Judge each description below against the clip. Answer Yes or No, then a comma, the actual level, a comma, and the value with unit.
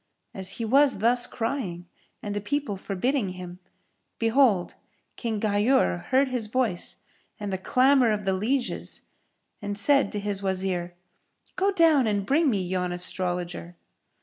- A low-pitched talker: No, high, 205 Hz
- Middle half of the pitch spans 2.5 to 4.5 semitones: No, wide, 5.4 semitones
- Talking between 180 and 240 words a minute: No, average, 145 wpm